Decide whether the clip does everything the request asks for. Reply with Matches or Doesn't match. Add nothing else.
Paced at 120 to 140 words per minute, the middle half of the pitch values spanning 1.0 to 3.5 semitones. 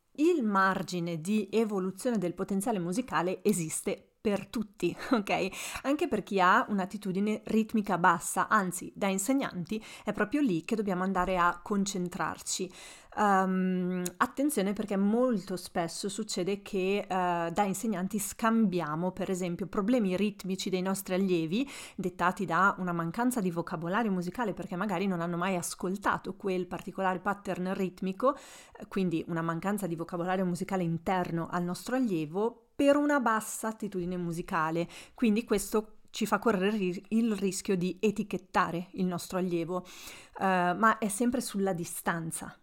Matches